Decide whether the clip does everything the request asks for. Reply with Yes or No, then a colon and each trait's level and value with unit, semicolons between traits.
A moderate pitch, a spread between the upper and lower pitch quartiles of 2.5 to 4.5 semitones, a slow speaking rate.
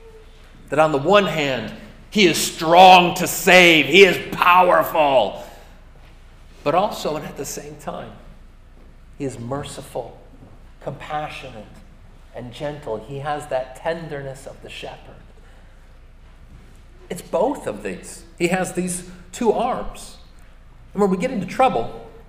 No: medium, 155 Hz; average, 5.3 semitones; slow, 130 wpm